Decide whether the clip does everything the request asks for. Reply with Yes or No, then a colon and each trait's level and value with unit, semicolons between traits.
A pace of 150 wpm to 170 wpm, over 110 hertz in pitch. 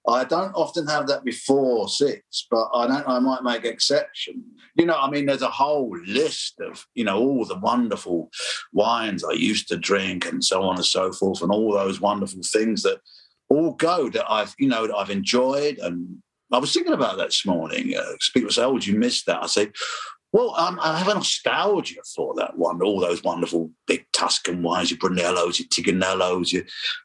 No: average, 200 wpm; low, 135 Hz